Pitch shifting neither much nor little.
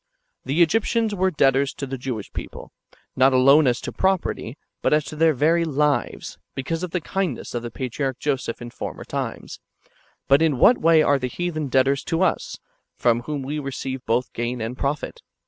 Yes: average, 4.0 semitones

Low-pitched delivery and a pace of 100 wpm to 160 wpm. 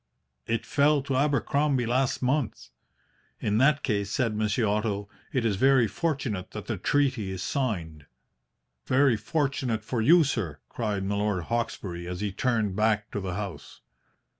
Yes: low, 110 Hz; average, 150 wpm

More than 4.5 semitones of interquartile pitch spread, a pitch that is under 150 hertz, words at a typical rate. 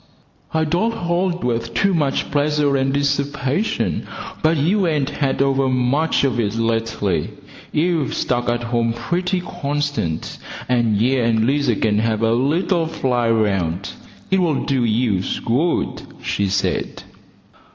No: average, 5.1 semitones; low, 135 Hz; slow, 130 wpm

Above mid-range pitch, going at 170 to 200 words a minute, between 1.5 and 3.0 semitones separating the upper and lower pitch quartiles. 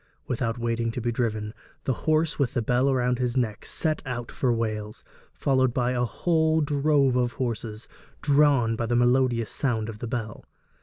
No: low, 125 Hz; average, 175 wpm; average, 2.7 semitones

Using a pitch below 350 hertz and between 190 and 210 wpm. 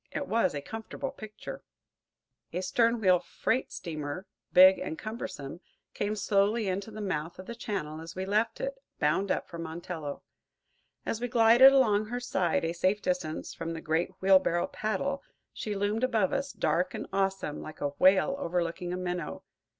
No: high, 190 Hz; average, 170 wpm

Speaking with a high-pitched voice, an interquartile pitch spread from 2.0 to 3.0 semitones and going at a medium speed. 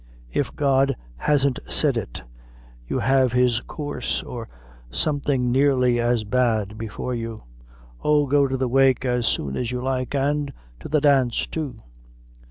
No: low, 130 Hz; average, 2.7 semitones; average, 150 wpm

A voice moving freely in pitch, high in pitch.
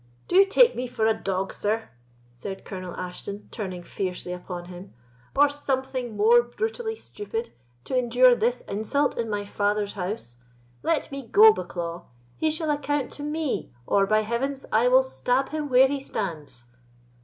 Yes: wide, 6.3 semitones; high, 235 Hz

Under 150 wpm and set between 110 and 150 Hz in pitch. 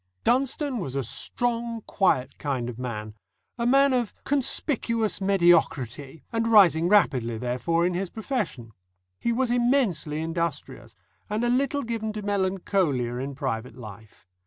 No: slow, 135 wpm; high, 190 Hz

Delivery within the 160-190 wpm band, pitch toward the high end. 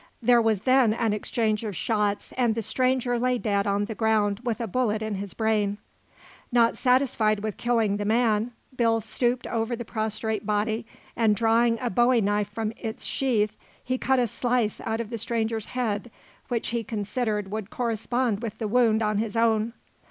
Yes: average, 180 wpm; high, 225 Hz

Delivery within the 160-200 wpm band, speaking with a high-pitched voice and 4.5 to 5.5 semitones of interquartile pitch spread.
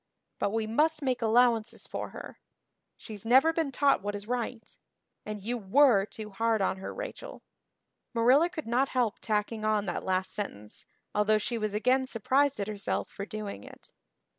No: average, 170 wpm; high, 225 Hz; average, 3.7 semitones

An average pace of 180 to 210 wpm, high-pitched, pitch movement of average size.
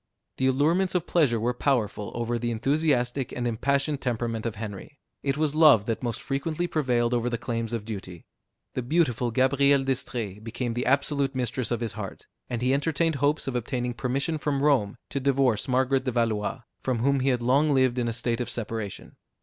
No: average, 190 wpm; low, 125 Hz; average, 3.1 semitones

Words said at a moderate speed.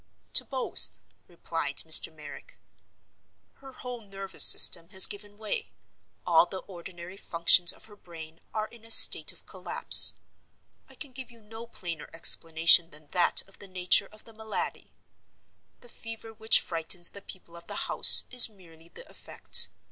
Yes: average, 160 wpm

